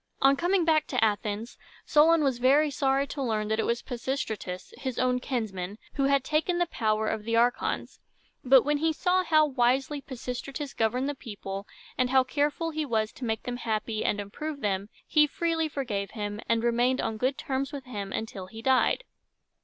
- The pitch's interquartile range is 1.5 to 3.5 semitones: No, average, 4.6 semitones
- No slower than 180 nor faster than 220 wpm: Yes, average, 190 wpm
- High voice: Yes, very high, 255 Hz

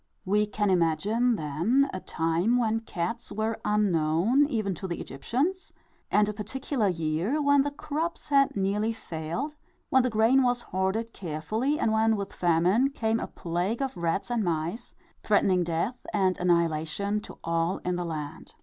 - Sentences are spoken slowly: No, average, 160 wpm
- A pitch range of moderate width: No, wide, 5.9 semitones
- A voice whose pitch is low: No, high, 210 Hz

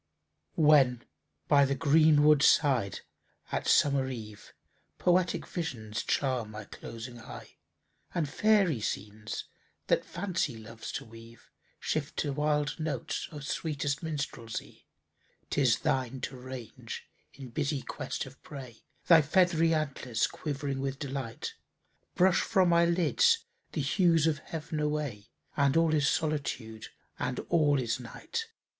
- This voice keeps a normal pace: No, slow, 130 wpm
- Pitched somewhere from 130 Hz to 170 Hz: Yes, medium, 140 Hz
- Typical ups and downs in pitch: Yes, average, 4.2 semitones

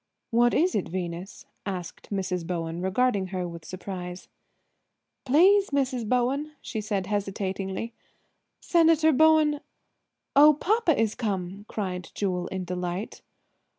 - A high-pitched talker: Yes, high, 205 Hz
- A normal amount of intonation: No, wide, 7.3 semitones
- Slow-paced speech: Yes, slow, 115 wpm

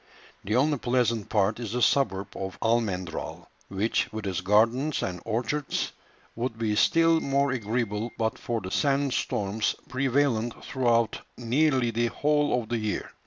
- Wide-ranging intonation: No, average, 3.8 semitones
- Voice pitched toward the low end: Yes, low, 115 Hz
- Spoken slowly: No, average, 150 wpm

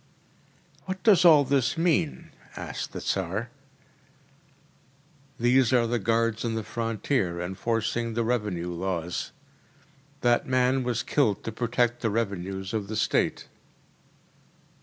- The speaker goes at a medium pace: No, slow, 120 wpm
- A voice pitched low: Yes, low, 115 Hz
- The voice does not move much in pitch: No, average, 3.5 semitones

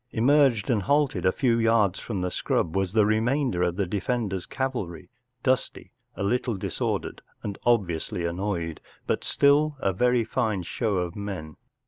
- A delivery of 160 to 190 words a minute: No, average, 150 wpm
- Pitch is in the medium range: No, low, 105 Hz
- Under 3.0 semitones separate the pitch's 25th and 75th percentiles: No, average, 5.2 semitones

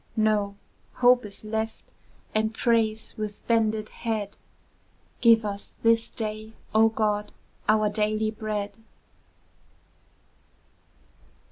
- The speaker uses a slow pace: Yes, slow, 95 wpm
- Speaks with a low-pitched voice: No, high, 215 Hz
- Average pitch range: No, narrow, 0.9 semitones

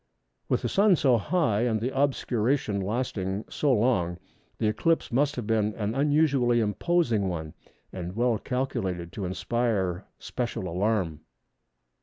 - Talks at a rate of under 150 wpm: Yes, slow, 135 wpm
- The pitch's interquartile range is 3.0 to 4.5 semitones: No, average, 5.1 semitones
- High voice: No, low, 115 Hz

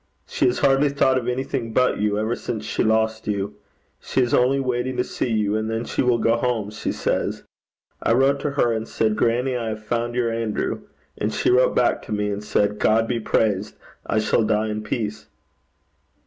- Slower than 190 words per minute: No, fast, 205 wpm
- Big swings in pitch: No, narrow, 2.5 semitones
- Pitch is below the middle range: Yes, low, 115 Hz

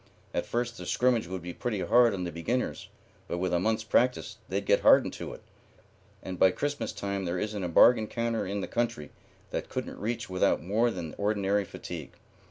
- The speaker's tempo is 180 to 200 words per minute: Yes, average, 195 wpm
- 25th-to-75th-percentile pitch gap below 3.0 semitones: No, average, 4.2 semitones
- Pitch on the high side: No, low, 100 Hz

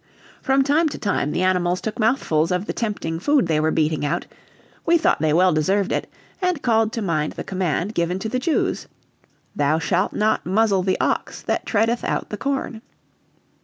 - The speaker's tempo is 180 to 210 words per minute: Yes, average, 190 wpm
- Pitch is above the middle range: Yes, high, 195 Hz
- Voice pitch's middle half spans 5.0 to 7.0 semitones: Yes, wide, 5.4 semitones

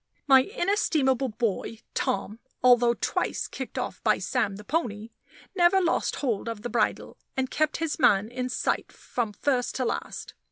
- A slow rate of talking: No, average, 160 wpm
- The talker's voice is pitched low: No, very high, 250 Hz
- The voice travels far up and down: No, average, 4.7 semitones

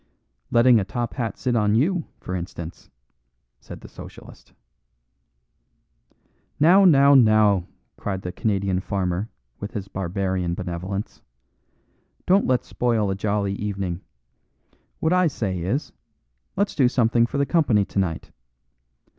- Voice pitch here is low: Yes, low, 105 Hz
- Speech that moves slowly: Yes, slow, 125 wpm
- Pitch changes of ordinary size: Yes, average, 4.8 semitones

